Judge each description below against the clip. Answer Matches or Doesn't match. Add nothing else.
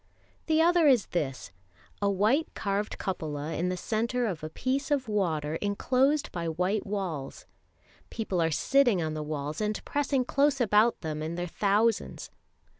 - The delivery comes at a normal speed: Matches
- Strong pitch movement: Matches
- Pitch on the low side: Doesn't match